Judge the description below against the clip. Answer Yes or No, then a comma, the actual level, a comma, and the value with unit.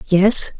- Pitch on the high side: Yes, high, 195 Hz